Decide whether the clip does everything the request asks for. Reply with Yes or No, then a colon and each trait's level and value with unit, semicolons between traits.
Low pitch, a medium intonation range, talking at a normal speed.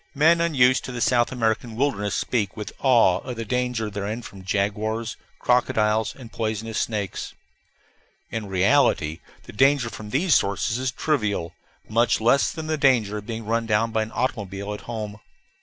Yes: low, 115 Hz; average, 3.2 semitones; average, 165 wpm